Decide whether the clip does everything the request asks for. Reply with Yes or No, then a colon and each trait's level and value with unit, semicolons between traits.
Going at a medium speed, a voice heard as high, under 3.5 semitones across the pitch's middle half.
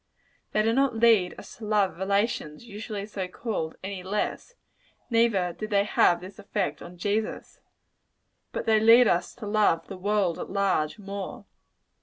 Yes: average, 160 wpm; high, 205 Hz; average, 2.9 semitones